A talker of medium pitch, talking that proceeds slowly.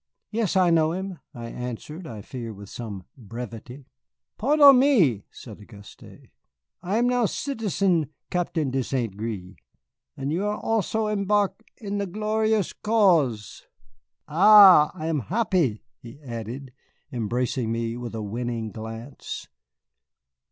Yes: medium, 145 Hz; slow, 130 wpm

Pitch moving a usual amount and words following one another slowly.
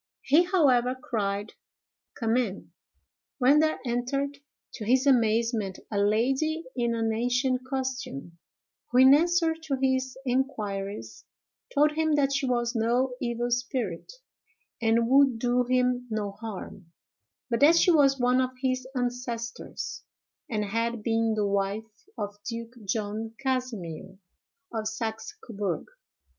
Yes: average, 3.2 semitones; slow, 130 wpm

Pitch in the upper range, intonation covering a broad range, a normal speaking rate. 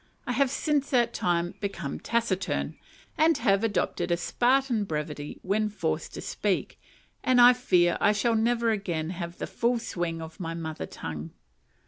Yes: high, 200 Hz; wide, 5.8 semitones; average, 160 wpm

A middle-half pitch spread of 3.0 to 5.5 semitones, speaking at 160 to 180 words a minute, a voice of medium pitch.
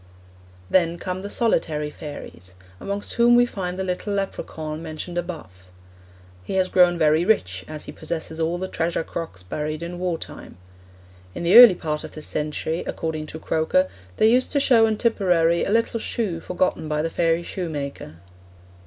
Yes: average, 3.5 semitones; average, 170 wpm; medium, 170 Hz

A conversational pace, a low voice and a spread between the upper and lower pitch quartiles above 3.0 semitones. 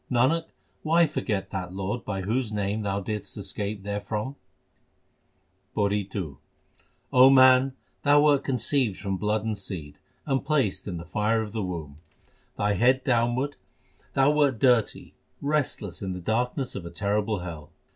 Yes: average, 150 wpm; low, 105 Hz; average, 4.9 semitones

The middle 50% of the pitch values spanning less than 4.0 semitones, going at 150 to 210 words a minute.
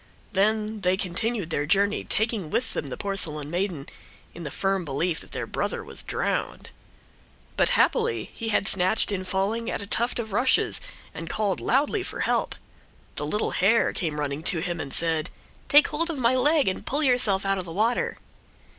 No: average, 5.0 semitones; average, 185 wpm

